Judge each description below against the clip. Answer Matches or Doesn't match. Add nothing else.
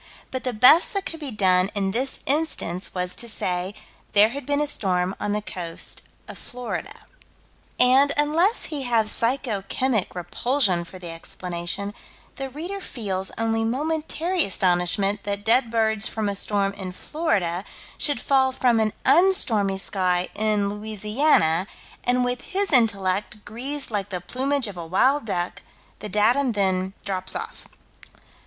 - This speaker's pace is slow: Doesn't match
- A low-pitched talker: Doesn't match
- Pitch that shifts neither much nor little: Doesn't match